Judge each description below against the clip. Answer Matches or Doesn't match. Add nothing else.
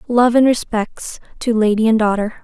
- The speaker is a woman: Matches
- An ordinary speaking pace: Matches